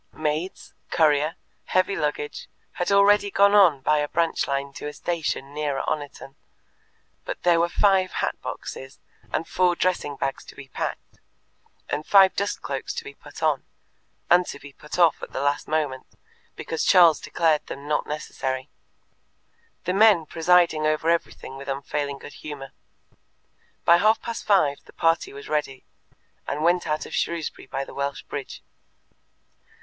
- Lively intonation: No, average, 3.7 semitones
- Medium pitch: Yes, medium, 155 Hz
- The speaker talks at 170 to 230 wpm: No, average, 160 wpm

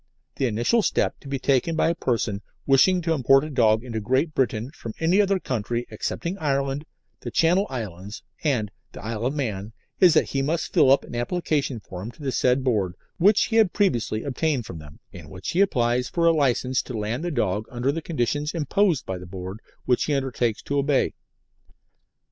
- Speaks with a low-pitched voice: Yes, low, 130 Hz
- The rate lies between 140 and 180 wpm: No, average, 200 wpm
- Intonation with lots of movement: Yes, wide, 5.7 semitones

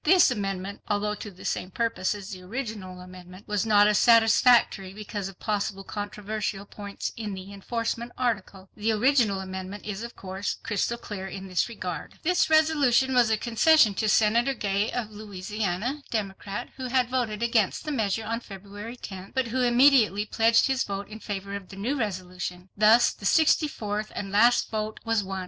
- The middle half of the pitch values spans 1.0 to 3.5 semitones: Yes, average, 3.2 semitones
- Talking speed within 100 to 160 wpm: No, average, 180 wpm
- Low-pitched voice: No, high, 210 Hz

